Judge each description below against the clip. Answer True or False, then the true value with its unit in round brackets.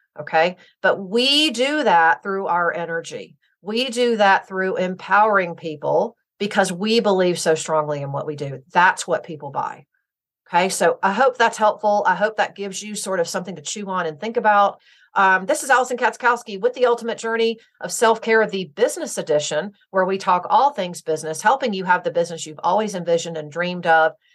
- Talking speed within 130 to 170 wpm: False (195 wpm)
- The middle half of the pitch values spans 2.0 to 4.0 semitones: False (4.9 semitones)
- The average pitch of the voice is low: False (195 Hz)